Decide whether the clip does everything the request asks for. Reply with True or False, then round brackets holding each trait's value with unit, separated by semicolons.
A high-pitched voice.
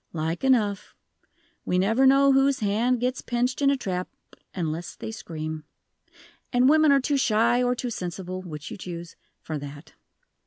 True (220 Hz)